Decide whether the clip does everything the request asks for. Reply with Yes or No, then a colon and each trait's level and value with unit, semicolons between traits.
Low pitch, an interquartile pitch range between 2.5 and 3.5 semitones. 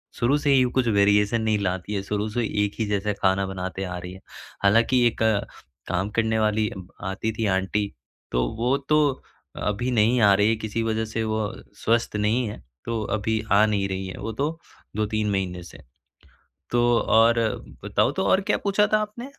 Yes: low, 110 Hz; average, 2.8 semitones